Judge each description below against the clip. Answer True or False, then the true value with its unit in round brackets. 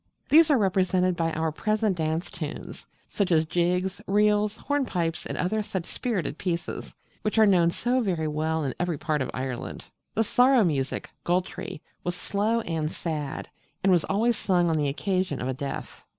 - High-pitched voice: False (180 Hz)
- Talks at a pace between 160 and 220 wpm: True (170 wpm)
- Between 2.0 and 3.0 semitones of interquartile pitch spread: False (4.7 semitones)